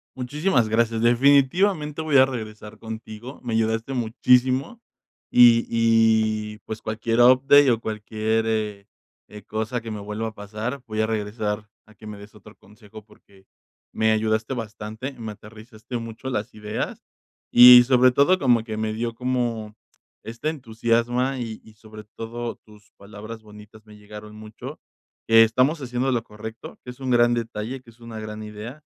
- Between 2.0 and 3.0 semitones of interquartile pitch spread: Yes, narrow, 2.4 semitones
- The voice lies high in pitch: No, low, 115 Hz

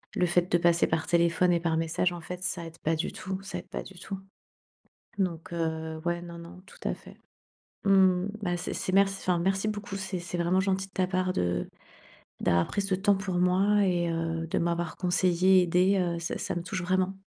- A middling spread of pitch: No, narrow, 1.9 semitones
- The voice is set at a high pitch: No, medium, 180 Hz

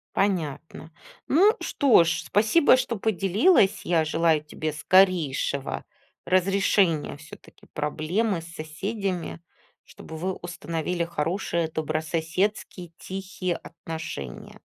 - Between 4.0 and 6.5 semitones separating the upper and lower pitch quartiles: No, average, 3.6 semitones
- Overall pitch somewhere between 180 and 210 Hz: No, medium, 170 Hz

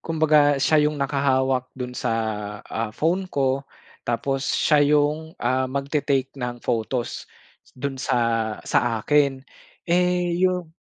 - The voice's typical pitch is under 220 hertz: Yes, medium, 140 Hz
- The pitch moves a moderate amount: Yes, average, 3.1 semitones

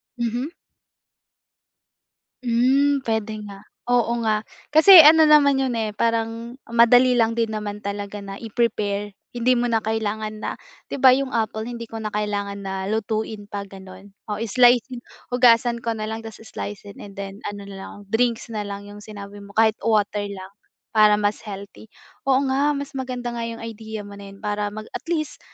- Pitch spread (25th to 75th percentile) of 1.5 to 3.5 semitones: Yes, average, 2.9 semitones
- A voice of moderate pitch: No, high, 220 Hz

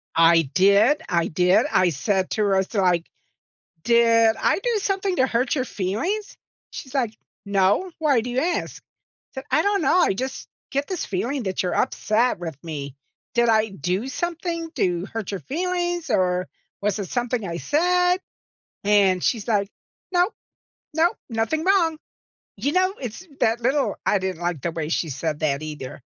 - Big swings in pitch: Yes, wide, 9.0 semitones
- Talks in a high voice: Yes, high, 225 Hz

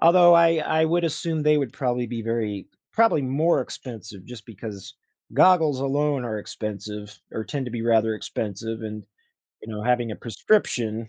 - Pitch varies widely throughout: Yes, wide, 5.7 semitones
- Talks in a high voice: No, low, 120 Hz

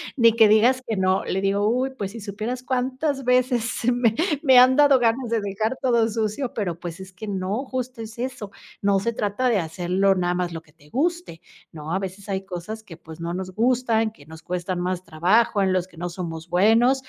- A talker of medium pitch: No, high, 210 Hz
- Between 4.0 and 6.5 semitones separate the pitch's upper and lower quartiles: Yes, average, 5.0 semitones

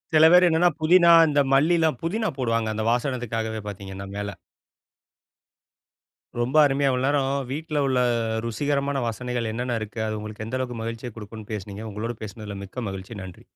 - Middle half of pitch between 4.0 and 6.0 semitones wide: Yes, average, 4.7 semitones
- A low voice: Yes, low, 120 Hz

